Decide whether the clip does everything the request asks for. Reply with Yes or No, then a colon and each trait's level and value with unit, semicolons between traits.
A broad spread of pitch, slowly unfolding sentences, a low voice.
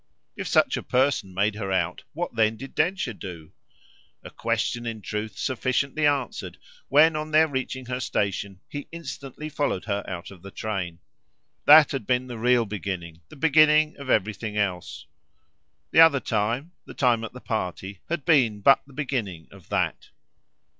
No: wide, 6.2 semitones; average, 165 wpm; low, 120 Hz